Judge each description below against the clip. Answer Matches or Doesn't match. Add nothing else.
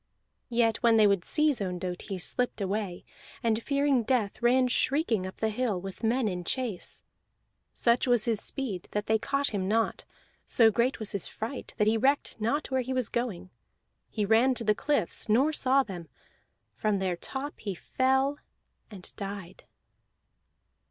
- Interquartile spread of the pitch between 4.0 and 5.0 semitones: Matches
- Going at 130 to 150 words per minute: Doesn't match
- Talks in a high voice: Matches